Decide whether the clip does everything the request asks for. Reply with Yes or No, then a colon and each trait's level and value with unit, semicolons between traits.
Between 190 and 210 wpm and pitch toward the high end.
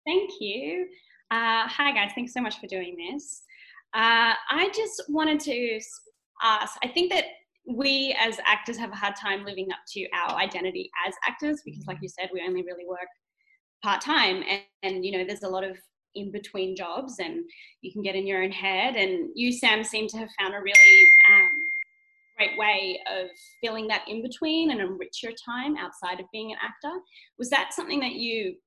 Yes: average, 195 wpm; high, 235 Hz